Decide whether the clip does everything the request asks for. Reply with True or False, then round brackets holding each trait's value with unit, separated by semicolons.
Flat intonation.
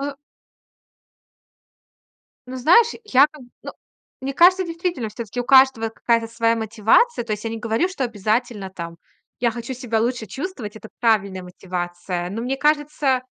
False (4.0 semitones)